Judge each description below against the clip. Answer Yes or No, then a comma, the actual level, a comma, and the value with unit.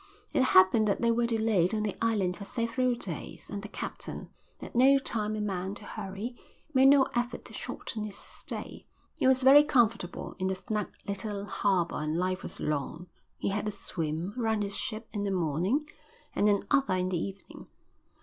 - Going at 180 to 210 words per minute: Yes, average, 190 wpm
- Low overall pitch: No, high, 210 Hz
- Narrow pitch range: No, average, 3.7 semitones